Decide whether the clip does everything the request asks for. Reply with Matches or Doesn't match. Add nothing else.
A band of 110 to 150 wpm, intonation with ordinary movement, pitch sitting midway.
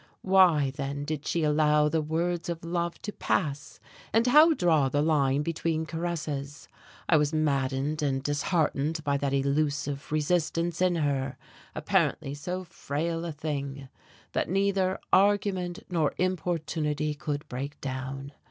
Matches